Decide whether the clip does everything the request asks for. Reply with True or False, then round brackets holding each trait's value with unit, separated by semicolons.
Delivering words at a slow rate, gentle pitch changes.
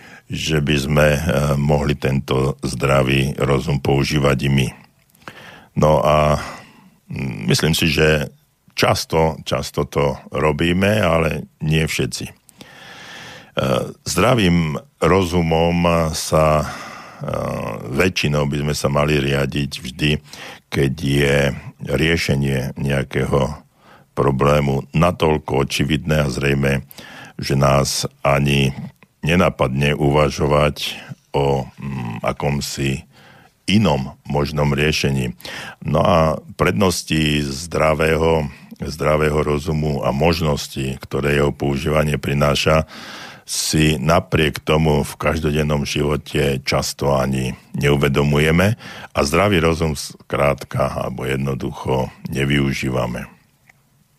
True (90 wpm; 1.9 semitones)